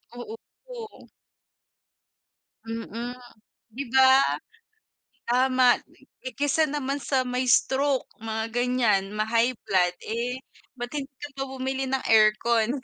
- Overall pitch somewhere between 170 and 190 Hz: No, very high, 250 Hz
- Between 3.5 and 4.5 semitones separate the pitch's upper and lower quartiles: No, average, 2.7 semitones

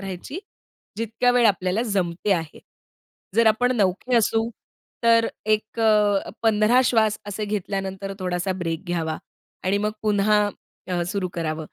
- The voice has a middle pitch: No, high, 205 Hz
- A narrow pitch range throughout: No, average, 3.3 semitones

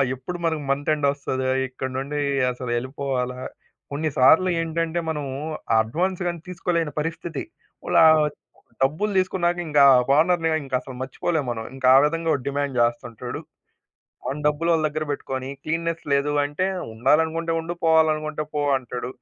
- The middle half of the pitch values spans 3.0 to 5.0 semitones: Yes, average, 3.8 semitones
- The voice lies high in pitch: No, medium, 150 Hz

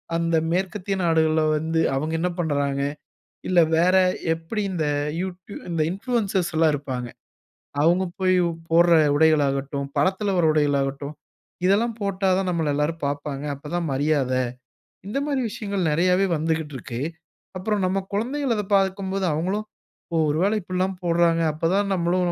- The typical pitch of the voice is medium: Yes, medium, 170 Hz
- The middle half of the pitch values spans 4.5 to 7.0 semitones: No, average, 3.9 semitones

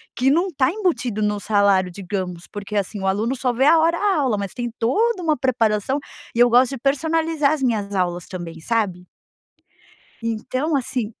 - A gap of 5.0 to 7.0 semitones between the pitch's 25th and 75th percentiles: Yes, wide, 5.6 semitones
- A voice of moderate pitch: No, high, 235 Hz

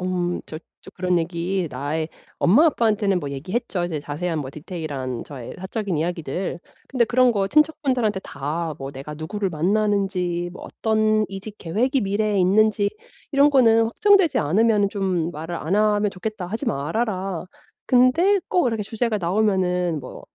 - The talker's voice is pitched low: No, high, 195 Hz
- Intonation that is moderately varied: Yes, average, 4.6 semitones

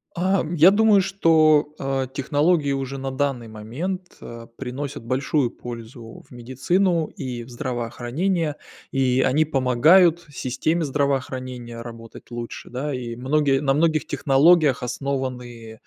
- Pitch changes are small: No, average, 4.1 semitones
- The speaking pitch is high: No, low, 135 Hz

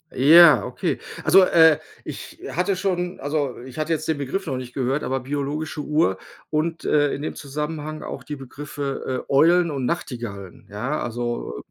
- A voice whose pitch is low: No, medium, 145 Hz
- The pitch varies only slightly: No, average, 3.5 semitones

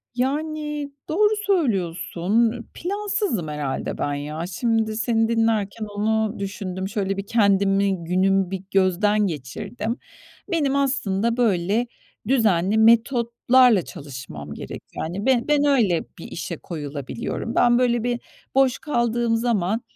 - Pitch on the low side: No, high, 220 Hz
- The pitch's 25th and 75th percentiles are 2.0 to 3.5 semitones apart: No, average, 4.5 semitones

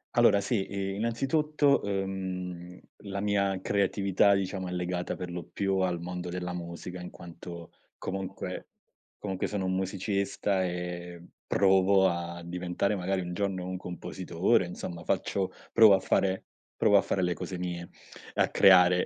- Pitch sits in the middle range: No, very low, 95 Hz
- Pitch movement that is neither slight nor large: No, narrow, 1.8 semitones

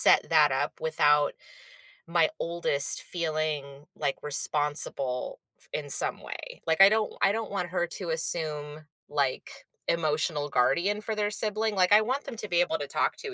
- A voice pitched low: No, medium, 170 Hz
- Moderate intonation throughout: No, wide, 5.8 semitones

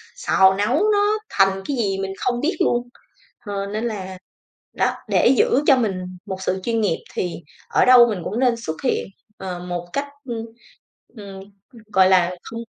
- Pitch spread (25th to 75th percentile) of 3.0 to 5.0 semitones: Yes, average, 4.4 semitones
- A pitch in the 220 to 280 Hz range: No, high, 205 Hz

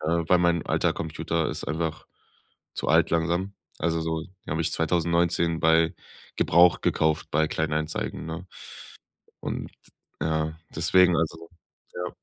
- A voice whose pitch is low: Yes, very low, 80 Hz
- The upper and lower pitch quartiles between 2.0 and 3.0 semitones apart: No, narrow, 1.2 semitones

